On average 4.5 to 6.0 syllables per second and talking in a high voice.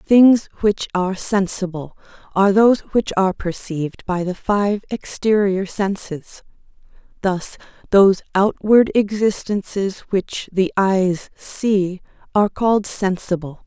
No: 4.1 syllables/s; high, 195 Hz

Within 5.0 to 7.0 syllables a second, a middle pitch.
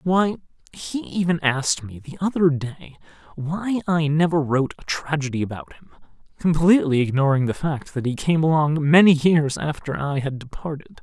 Yes: 5.1 syllables/s; medium, 155 Hz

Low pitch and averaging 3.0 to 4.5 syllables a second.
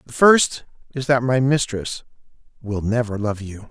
Yes: low, 120 Hz; 4.4 syllables/s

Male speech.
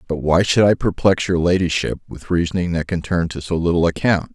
Yes: male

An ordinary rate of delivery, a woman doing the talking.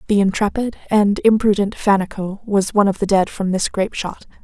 Yes: average, 190 wpm; female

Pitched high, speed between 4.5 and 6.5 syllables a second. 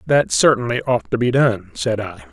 No: low, 120 Hz; 4.9 syllables/s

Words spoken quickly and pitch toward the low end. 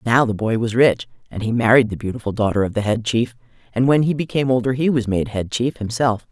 Yes: fast, 245 wpm; low, 120 Hz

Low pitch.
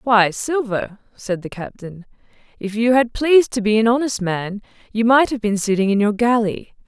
No: high, 220 Hz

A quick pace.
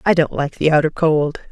Yes: fast, 240 wpm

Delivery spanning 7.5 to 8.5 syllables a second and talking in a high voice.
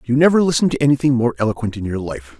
No: 7.6 syllables/s; low, 125 Hz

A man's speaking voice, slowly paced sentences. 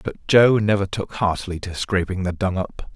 No: male; fast, 205 wpm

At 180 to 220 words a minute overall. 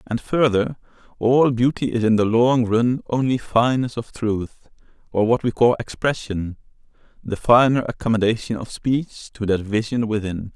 No: average, 155 wpm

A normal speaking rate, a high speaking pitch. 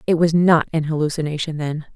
No: average, 185 wpm; medium, 155 Hz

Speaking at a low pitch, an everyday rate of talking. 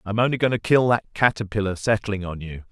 No: low, 105 Hz; fast, 245 wpm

